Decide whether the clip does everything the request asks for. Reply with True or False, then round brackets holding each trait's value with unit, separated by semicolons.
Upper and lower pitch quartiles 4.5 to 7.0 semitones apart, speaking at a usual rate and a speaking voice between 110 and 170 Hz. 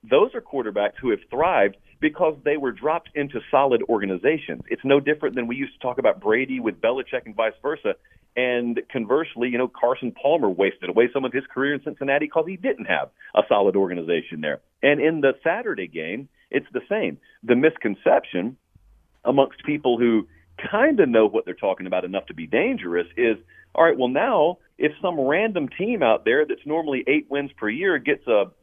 True (5.2 semitones; 195 wpm; 140 Hz)